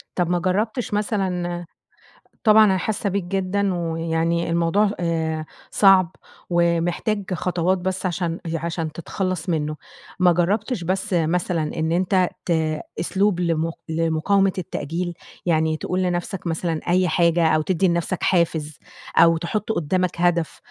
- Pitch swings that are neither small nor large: No, narrow, 2.2 semitones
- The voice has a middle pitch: Yes, medium, 175 Hz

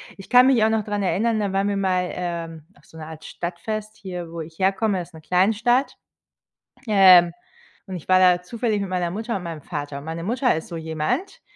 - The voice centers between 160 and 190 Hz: Yes, medium, 185 Hz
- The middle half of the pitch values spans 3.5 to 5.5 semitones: Yes, average, 4.1 semitones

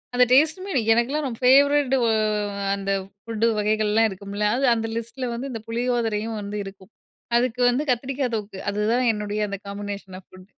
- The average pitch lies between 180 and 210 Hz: No, high, 225 Hz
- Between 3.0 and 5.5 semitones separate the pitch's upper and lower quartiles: Yes, average, 3.3 semitones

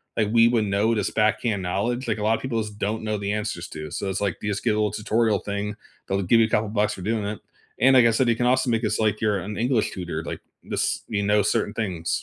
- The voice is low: Yes, low, 105 Hz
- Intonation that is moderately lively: No, narrow, 2.0 semitones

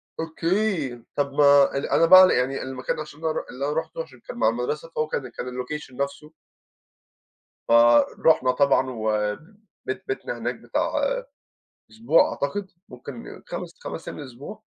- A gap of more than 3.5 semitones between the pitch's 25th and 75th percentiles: Yes, average, 4.3 semitones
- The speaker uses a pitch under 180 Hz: Yes, medium, 140 Hz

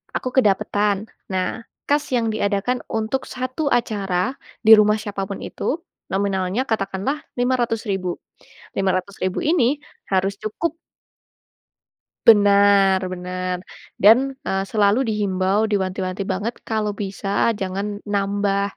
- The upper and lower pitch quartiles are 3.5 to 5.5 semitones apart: No, narrow, 2.6 semitones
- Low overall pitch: No, high, 205 Hz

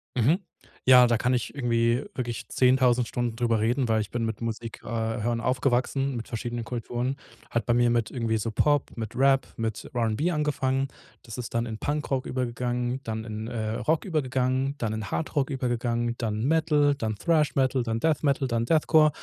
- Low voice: Yes, low, 120 Hz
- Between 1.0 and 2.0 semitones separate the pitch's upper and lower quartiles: No, average, 2.8 semitones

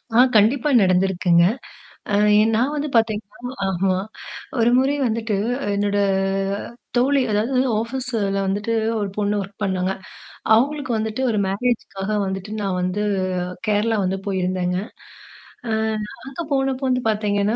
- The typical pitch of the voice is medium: No, high, 210 Hz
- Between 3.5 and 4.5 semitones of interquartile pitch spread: Yes, average, 4.0 semitones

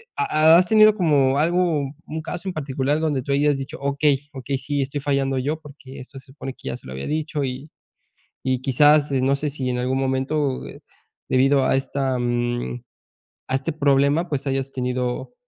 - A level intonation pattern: Yes, narrow, 2.2 semitones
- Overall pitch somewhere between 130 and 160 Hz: Yes, medium, 140 Hz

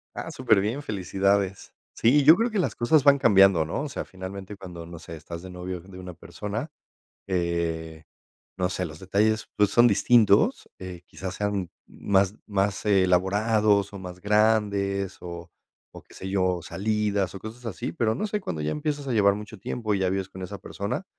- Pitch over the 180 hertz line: No, low, 100 Hz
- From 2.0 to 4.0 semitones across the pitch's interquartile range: Yes, average, 2.9 semitones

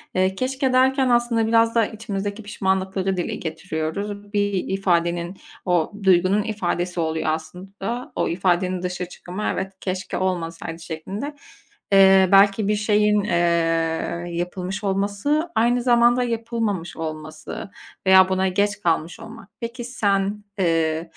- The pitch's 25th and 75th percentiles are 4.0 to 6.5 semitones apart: No, average, 3.6 semitones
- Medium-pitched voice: No, high, 195 Hz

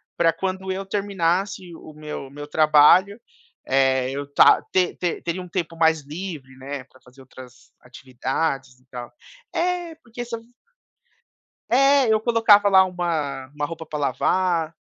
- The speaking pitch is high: No, medium, 165 Hz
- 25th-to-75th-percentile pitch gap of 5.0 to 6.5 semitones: Yes, wide, 5.6 semitones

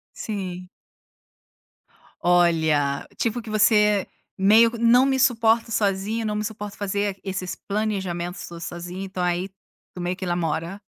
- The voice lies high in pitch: Yes, high, 195 Hz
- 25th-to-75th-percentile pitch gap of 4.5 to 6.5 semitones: No, average, 3.6 semitones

